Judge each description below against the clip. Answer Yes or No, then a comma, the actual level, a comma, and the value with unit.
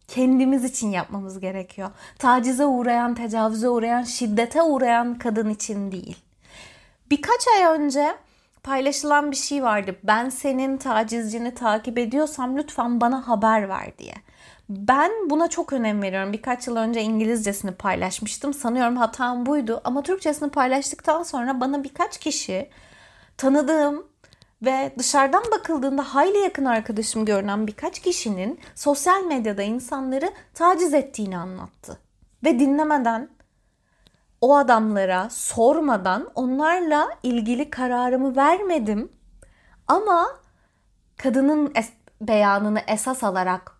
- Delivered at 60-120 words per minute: Yes, average, 110 wpm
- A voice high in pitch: Yes, very high, 255 Hz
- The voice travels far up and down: No, average, 4.8 semitones